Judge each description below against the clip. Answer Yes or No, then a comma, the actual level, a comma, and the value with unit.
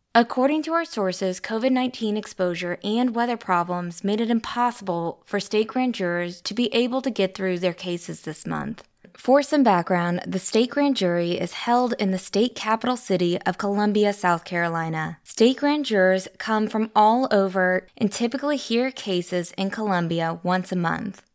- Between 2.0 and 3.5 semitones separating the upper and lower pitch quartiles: No, average, 4.8 semitones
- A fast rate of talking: No, average, 170 wpm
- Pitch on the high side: Yes, high, 205 Hz